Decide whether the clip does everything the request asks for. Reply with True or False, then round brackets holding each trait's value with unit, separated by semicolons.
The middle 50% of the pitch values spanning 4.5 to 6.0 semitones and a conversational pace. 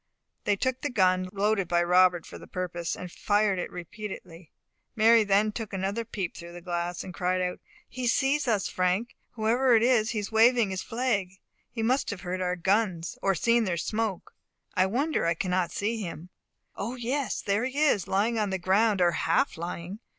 False (3.9 semitones; 195 wpm)